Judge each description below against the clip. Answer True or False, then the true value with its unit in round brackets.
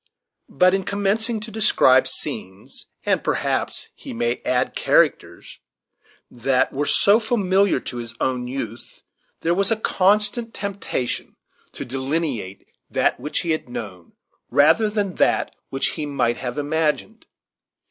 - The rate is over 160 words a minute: False (135 wpm)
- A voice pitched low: False (150 Hz)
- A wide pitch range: True (8.2 semitones)